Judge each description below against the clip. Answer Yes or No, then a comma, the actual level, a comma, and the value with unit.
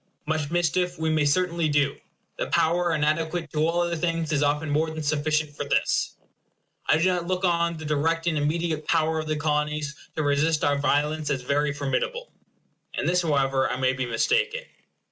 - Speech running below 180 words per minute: No, average, 185 wpm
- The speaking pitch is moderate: Yes, medium, 155 Hz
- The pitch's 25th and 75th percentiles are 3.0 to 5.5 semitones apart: No, narrow, 2.5 semitones